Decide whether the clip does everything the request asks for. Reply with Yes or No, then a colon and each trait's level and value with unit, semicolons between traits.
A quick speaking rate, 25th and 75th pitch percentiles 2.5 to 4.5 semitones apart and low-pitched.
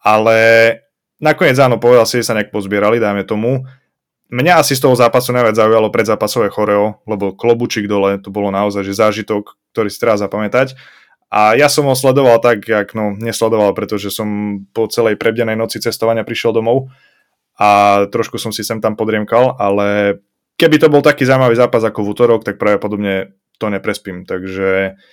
Yes: fast, 170 wpm; average, 2.8 semitones; low, 110 Hz